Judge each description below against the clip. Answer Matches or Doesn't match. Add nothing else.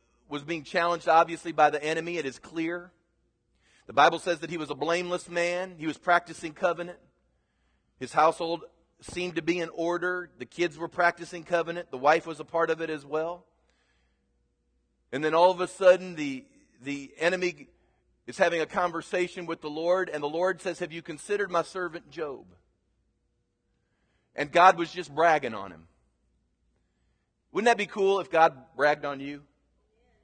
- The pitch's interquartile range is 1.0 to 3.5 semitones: Matches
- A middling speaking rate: Matches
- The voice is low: Doesn't match